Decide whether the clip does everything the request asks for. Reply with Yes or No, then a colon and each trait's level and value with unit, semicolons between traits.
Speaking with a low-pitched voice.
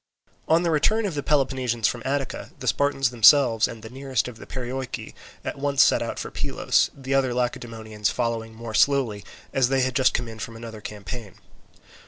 Yes: low, 125 Hz